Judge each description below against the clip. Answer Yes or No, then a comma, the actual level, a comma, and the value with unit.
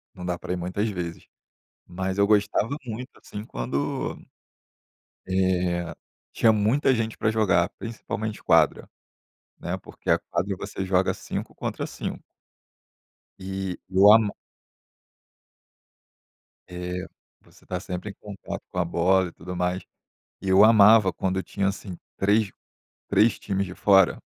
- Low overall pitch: Yes, very low, 95 Hz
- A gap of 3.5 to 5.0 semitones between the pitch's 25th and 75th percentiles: No, average, 2.7 semitones